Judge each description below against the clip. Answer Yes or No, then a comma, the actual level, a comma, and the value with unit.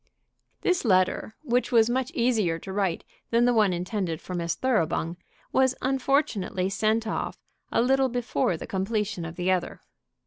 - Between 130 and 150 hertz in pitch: No, high, 215 Hz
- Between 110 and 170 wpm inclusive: Yes, average, 160 wpm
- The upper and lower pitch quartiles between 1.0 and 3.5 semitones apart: No, average, 5.2 semitones